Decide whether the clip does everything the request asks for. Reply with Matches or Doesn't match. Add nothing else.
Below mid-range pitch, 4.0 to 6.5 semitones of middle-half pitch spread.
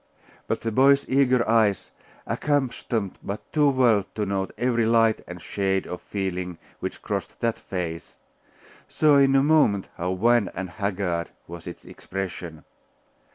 Matches